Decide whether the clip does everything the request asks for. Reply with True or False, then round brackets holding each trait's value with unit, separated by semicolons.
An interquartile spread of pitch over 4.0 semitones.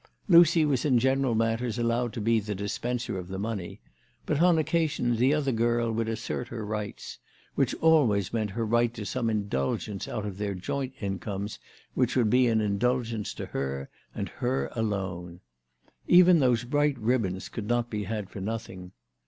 False (3.4 semitones)